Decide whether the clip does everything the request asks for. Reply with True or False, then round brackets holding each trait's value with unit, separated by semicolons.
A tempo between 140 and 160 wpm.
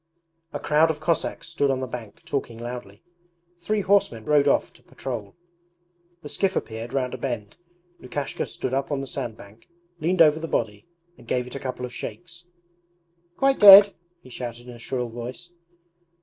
False (175 wpm)